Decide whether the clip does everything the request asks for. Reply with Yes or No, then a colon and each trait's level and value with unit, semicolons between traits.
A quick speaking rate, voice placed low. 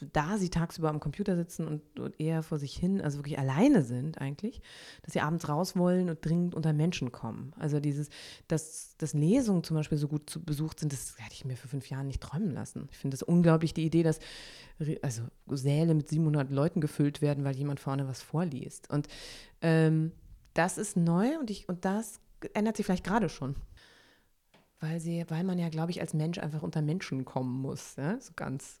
No: fast, 205 wpm; medium, 155 Hz